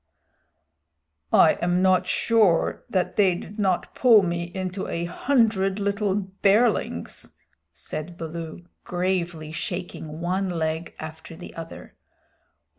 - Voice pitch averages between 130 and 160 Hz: No, medium, 180 Hz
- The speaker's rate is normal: No, slow, 115 wpm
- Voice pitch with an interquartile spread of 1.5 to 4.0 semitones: Yes, average, 2.7 semitones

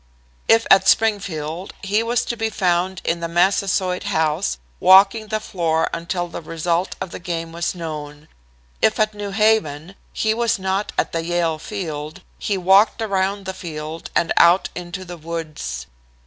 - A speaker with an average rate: Yes, average, 160 wpm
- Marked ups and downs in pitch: No, average, 3.4 semitones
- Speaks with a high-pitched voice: No, medium, 180 Hz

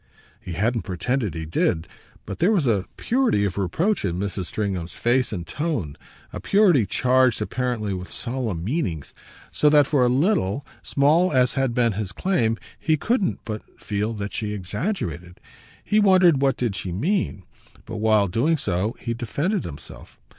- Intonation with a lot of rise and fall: Yes, wide, 7.0 semitones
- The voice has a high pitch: No, low, 115 Hz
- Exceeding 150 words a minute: Yes, average, 165 wpm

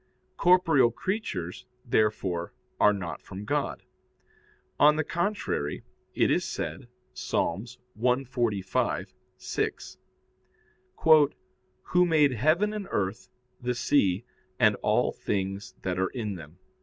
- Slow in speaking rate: Yes, slow, 105 wpm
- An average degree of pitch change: No, wide, 7.5 semitones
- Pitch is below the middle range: Yes, low, 120 Hz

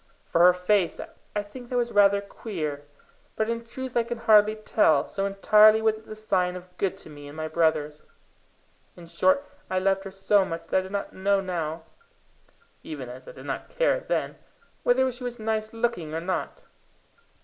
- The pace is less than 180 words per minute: No, average, 195 wpm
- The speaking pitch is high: Yes, high, 195 Hz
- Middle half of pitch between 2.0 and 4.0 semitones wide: No, average, 4.5 semitones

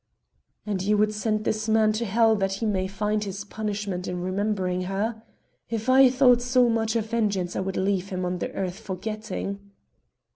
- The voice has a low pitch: No, high, 210 Hz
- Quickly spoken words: No, average, 185 wpm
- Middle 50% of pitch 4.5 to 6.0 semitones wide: No, narrow, 2.5 semitones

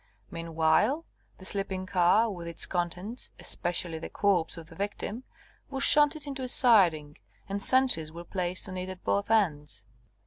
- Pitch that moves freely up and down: No, average, 4.9 semitones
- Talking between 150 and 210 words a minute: Yes, average, 160 wpm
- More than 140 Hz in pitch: Yes, medium, 185 Hz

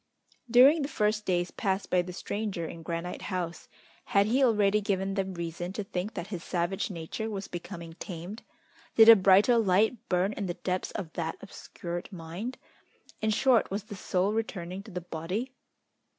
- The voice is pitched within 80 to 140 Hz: No, high, 195 Hz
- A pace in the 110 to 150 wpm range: No, average, 175 wpm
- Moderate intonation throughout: Yes, average, 3.4 semitones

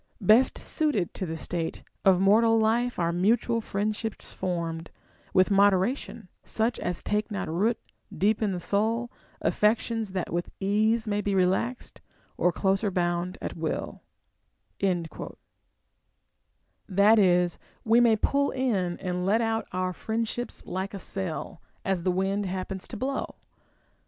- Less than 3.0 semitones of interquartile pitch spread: No, average, 3.5 semitones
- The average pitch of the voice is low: No, high, 200 Hz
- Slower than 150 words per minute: Yes, average, 140 wpm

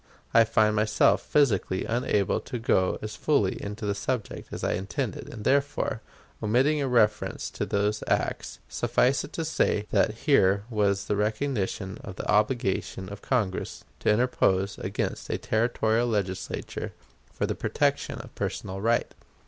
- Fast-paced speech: No, average, 150 wpm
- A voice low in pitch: Yes, low, 105 Hz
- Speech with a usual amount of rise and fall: Yes, average, 3.5 semitones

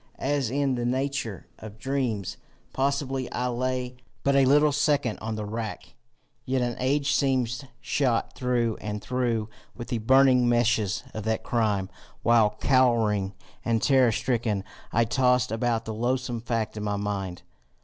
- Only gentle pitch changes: No, average, 3.1 semitones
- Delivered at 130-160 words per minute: Yes, average, 155 wpm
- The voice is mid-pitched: No, low, 120 Hz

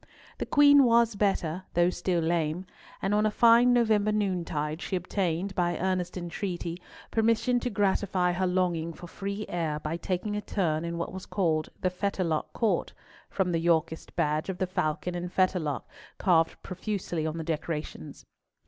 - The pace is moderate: Yes, average, 165 wpm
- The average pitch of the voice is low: No, medium, 180 Hz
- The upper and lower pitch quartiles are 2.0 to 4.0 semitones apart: Yes, average, 3.3 semitones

